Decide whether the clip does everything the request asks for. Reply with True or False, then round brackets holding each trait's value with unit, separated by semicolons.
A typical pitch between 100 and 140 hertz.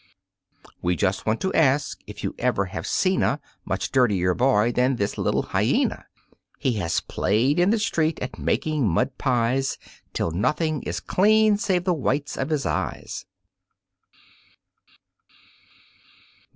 True (135 Hz)